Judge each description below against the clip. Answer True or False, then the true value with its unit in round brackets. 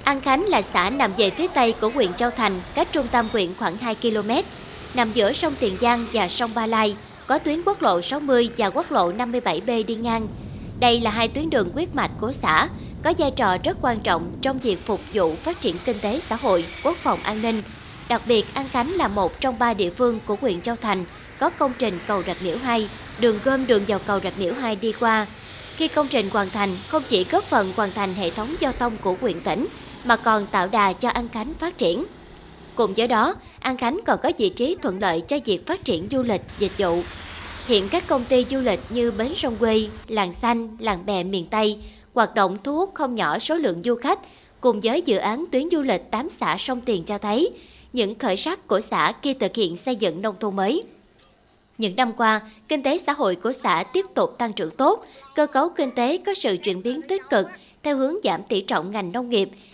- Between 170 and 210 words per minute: False (230 wpm)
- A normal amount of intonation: True (4.9 semitones)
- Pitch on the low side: False (235 Hz)